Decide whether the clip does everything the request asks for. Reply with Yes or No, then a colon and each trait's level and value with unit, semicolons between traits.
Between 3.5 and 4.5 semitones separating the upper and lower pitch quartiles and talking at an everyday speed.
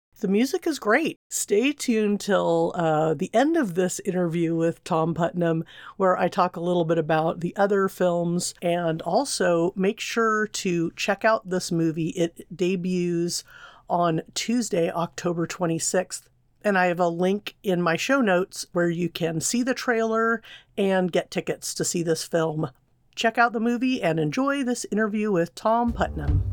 Yes: average, 4.2 semitones; average, 165 wpm